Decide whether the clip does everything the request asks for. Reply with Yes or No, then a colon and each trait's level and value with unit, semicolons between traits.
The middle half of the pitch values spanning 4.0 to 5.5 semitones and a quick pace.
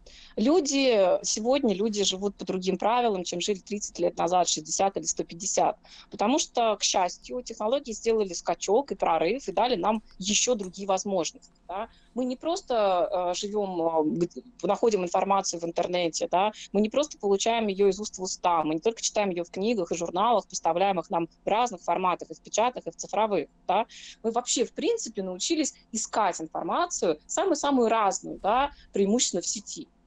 Yes: average, 4.4 semitones; fast, 170 wpm